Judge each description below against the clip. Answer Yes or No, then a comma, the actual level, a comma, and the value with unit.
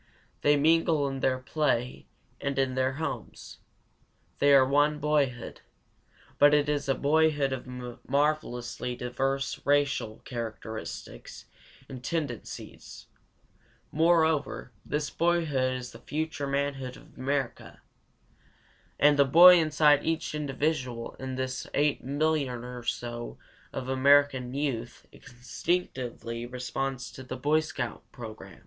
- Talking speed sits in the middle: No, slow, 115 wpm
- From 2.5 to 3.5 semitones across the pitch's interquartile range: Yes, average, 2.8 semitones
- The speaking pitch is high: No, low, 135 Hz